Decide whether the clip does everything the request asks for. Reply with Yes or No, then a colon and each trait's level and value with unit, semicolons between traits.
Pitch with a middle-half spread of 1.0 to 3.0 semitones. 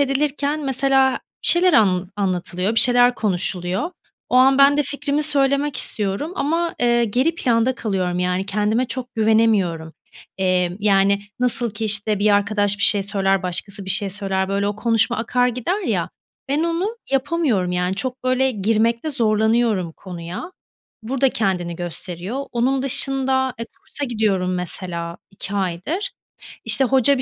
No: wide, 5.6 semitones